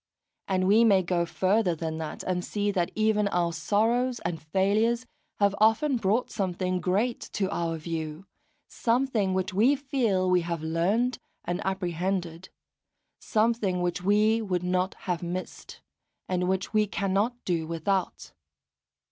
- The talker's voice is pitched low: No, high, 190 Hz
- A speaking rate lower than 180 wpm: Yes, average, 140 wpm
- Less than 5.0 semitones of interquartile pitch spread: Yes, average, 3.6 semitones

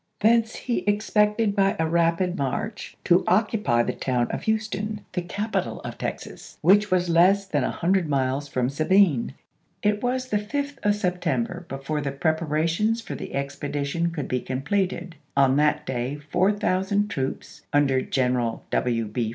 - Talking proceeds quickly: No, average, 160 wpm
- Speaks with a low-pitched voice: No, medium, 170 Hz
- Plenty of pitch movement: Yes, wide, 6.9 semitones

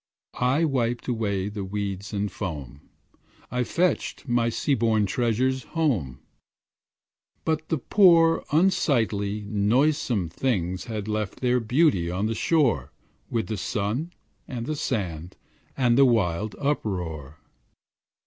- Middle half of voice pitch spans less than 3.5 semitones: No, average, 5.2 semitones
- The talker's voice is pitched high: No, low, 115 Hz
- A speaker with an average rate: No, slow, 120 wpm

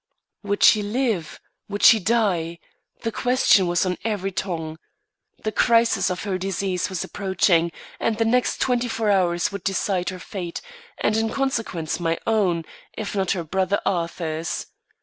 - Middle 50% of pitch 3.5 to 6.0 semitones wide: Yes, average, 4.0 semitones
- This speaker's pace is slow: No, average, 155 wpm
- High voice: Yes, high, 195 Hz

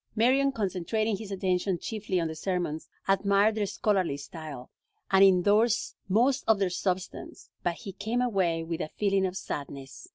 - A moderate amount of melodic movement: Yes, average, 3.6 semitones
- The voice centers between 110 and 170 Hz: No, high, 195 Hz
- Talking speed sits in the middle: Yes, average, 160 wpm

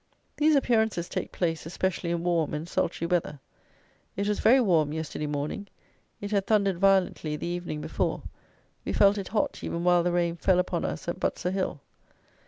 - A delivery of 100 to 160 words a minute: No, average, 180 wpm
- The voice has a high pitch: No, medium, 175 Hz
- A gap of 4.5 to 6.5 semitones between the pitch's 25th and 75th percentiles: No, average, 3.2 semitones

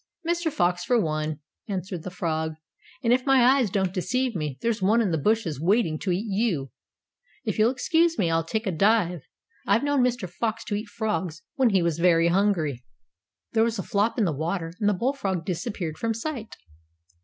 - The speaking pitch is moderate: No, high, 200 Hz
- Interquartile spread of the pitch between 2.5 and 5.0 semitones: No, wide, 5.5 semitones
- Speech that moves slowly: No, average, 195 wpm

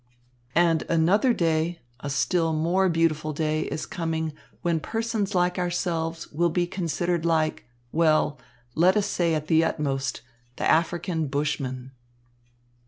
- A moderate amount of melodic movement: No, narrow, 2.1 semitones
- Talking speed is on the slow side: Yes, slow, 130 wpm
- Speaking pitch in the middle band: Yes, medium, 165 Hz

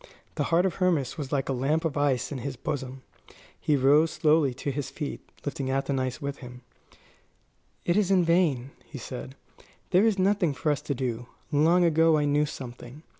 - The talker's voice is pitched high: No, medium, 145 Hz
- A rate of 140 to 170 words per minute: No, average, 185 wpm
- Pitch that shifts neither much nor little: Yes, average, 3.6 semitones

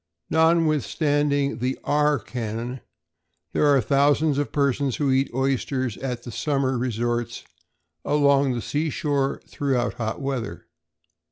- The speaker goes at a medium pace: No, slow, 115 wpm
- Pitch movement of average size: Yes, average, 3.0 semitones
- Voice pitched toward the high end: No, low, 135 Hz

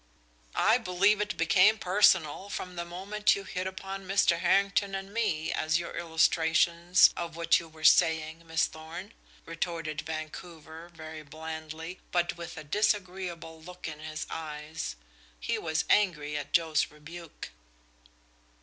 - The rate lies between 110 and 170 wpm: Yes, slow, 135 wpm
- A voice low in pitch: No, medium, 170 Hz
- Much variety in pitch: No, average, 2.8 semitones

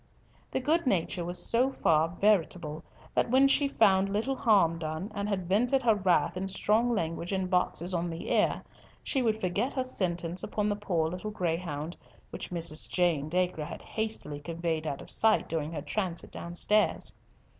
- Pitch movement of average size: Yes, average, 4.3 semitones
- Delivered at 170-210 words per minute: Yes, average, 175 wpm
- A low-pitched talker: No, medium, 185 Hz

